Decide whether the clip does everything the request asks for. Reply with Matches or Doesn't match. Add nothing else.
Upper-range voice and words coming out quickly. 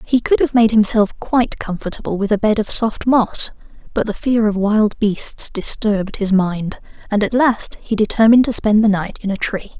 Matches